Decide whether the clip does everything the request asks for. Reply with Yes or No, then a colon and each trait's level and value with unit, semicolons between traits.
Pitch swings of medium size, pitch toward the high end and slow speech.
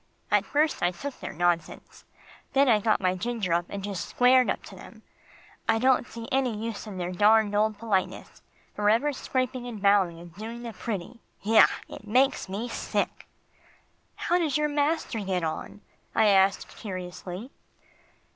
No: average, 4.6 semitones; high, 215 Hz; average, 165 wpm